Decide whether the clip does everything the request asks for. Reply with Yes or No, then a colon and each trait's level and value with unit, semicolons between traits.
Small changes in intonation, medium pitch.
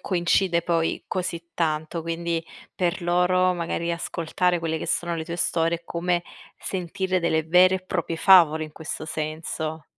Yes: narrow, 1.7 semitones; medium, 170 Hz